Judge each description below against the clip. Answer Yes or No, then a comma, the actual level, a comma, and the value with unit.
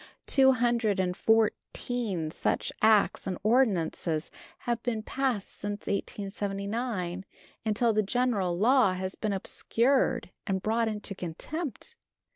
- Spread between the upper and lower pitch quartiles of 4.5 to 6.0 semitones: No, average, 4.0 semitones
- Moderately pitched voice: No, high, 215 Hz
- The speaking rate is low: Yes, slow, 115 wpm